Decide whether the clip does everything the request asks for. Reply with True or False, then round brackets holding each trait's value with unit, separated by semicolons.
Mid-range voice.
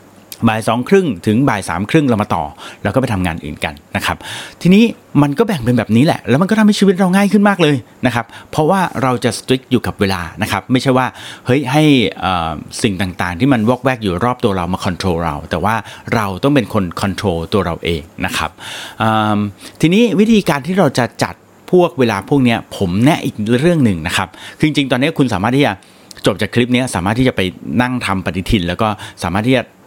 False (115 Hz)